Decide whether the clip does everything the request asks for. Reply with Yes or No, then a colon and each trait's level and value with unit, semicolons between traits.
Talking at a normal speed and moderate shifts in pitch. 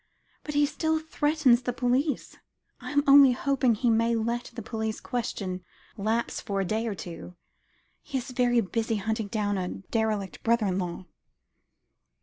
Yes: average, 160 wpm; average, 3.4 semitones